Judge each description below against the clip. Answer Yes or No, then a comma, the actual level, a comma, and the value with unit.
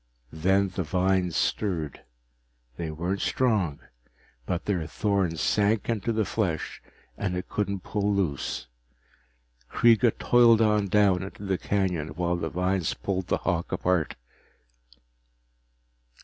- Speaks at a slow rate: Yes, slow, 120 wpm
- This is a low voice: Yes, very low, 95 Hz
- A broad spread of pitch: No, average, 2.9 semitones